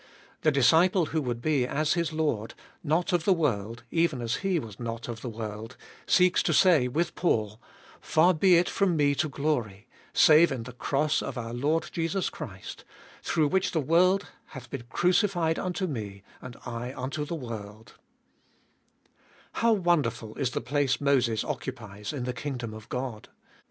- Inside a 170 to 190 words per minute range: Yes, average, 175 wpm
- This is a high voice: No, medium, 140 Hz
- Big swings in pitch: Yes, wide, 6.1 semitones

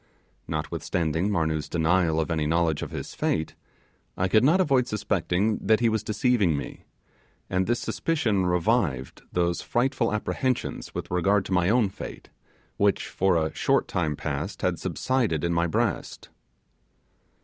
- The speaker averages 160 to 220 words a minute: No, average, 150 wpm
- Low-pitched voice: Yes, very low, 95 Hz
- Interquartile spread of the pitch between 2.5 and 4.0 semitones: No, average, 5.0 semitones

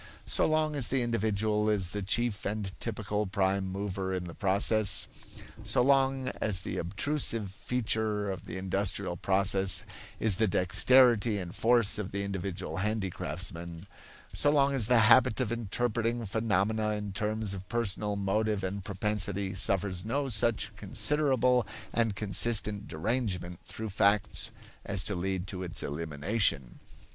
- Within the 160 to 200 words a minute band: No, average, 140 wpm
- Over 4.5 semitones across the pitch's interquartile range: No, average, 3.1 semitones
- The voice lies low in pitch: Yes, low, 105 Hz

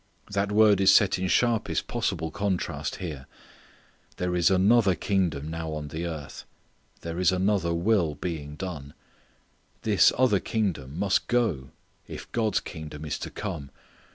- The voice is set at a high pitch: No, very low, 90 Hz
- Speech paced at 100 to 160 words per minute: Yes, average, 145 wpm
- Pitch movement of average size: Yes, average, 4.5 semitones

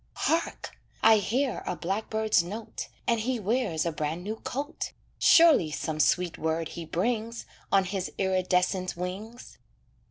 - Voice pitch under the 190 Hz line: No, high, 195 Hz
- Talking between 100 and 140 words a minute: Yes, slow, 135 wpm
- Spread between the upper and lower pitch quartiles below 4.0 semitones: No, average, 4.4 semitones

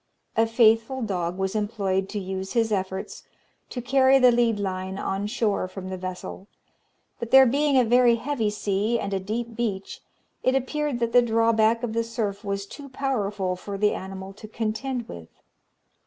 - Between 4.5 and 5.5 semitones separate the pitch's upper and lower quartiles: No, average, 3.6 semitones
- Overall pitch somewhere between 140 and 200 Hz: No, high, 220 Hz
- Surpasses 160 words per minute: Yes, average, 175 wpm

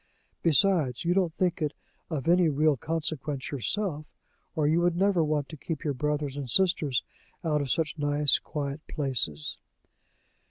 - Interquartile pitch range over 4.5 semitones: No, average, 2.9 semitones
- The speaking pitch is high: No, medium, 150 Hz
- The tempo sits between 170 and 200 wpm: No, average, 155 wpm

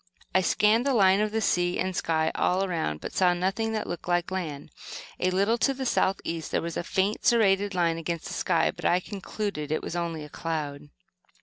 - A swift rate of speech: Yes, fast, 215 wpm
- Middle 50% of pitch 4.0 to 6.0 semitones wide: No, average, 3.5 semitones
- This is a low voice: No, medium, 185 Hz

